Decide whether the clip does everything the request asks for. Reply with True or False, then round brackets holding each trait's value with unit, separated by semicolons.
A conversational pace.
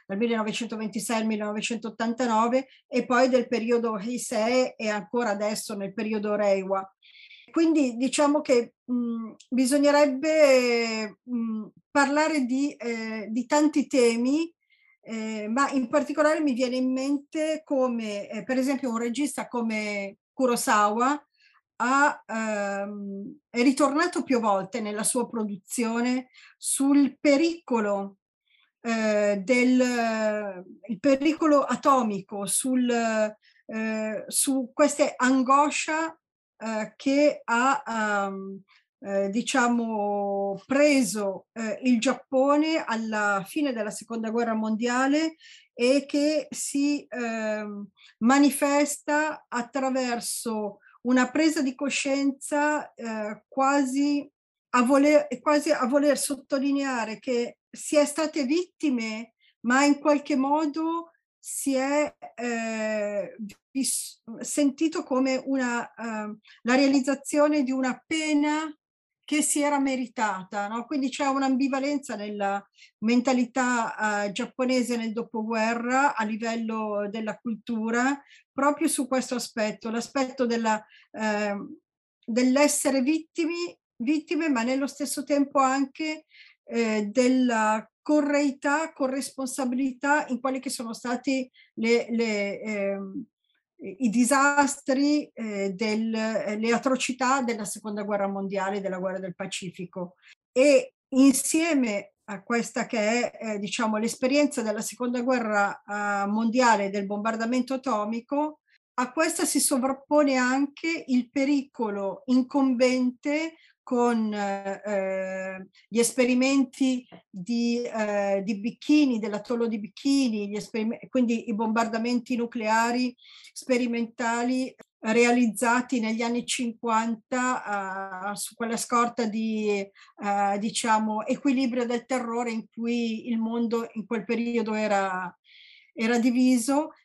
False (110 wpm)